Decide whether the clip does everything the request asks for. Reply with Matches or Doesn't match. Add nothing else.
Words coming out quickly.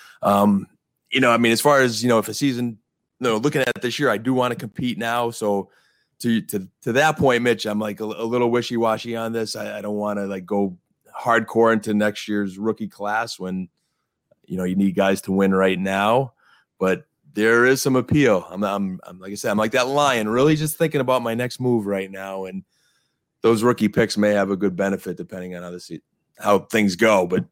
Matches